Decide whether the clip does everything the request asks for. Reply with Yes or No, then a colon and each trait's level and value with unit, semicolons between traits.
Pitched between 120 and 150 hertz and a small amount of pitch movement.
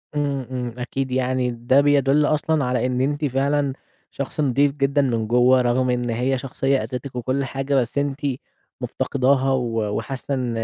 Yes: low, 130 Hz; narrow, 2.0 semitones